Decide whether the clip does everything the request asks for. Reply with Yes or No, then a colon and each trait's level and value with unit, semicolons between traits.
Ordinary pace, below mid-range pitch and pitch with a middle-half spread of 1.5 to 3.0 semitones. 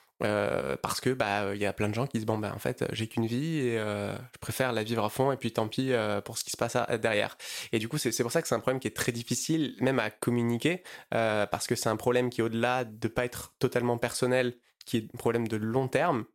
No: fast, 285 wpm; low, 120 Hz; narrow, 2.5 semitones